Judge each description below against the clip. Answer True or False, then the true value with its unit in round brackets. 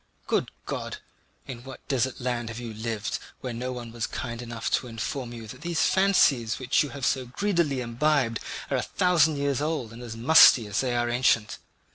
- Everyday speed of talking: True (195 wpm)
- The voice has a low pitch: True (125 Hz)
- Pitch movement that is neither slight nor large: True (3.3 semitones)